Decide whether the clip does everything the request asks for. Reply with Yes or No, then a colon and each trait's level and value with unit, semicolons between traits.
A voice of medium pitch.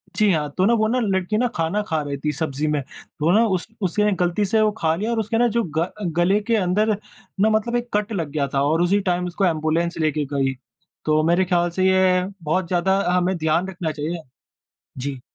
Yes: medium, 180 Hz